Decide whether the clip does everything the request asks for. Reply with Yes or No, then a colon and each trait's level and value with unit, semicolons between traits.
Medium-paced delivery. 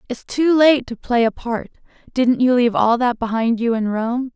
No: fast, 220 wpm